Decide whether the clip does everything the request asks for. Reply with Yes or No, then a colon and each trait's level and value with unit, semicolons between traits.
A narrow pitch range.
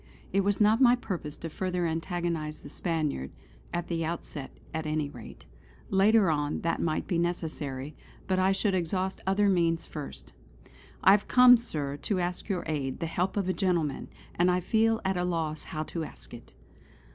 No: average, 3.5 semitones